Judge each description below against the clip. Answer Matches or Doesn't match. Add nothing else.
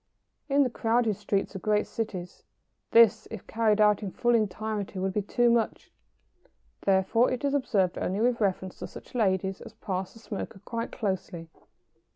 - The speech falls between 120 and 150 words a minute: Doesn't match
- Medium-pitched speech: Doesn't match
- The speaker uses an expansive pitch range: Doesn't match